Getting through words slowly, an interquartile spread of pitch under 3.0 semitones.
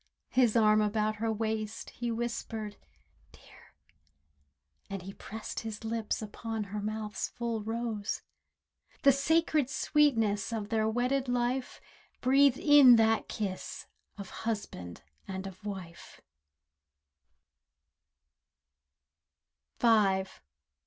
Yes: slow, 95 wpm; narrow, 2.5 semitones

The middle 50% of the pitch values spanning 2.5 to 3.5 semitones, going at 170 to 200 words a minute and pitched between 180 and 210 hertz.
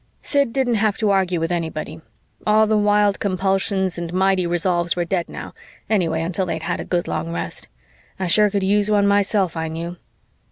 Yes: average, 3.2 semitones; average, 190 wpm; medium, 185 Hz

